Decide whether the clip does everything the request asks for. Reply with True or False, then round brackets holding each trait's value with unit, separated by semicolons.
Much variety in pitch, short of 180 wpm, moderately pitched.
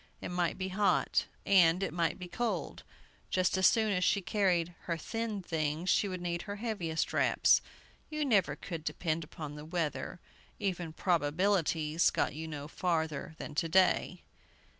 False (3.3 semitones; 160 wpm; 175 Hz)